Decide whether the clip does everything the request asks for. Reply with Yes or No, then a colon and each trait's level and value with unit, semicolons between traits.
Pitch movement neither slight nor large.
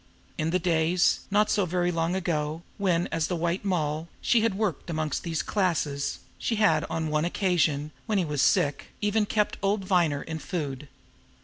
Yes: average, 3.8 semitones